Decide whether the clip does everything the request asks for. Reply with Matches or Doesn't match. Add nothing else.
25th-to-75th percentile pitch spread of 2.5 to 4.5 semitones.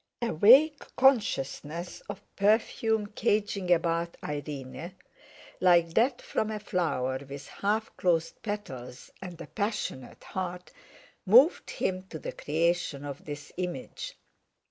Doesn't match